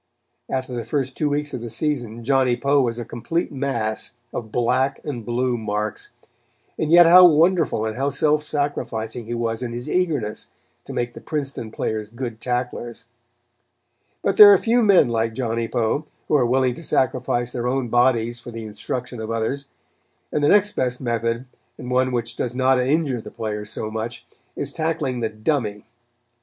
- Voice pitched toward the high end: No, low, 125 Hz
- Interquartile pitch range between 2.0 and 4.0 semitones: Yes, average, 3.5 semitones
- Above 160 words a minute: Yes, average, 180 wpm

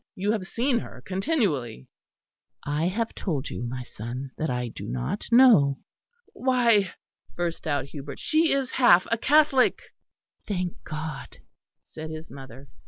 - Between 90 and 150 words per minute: Yes, average, 140 wpm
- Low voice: No, medium, 165 Hz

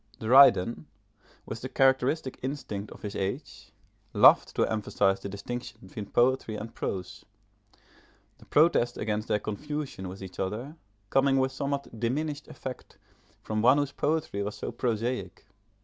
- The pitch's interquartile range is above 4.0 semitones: Yes, average, 4.5 semitones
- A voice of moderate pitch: No, low, 120 Hz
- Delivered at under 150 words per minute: Yes, average, 140 wpm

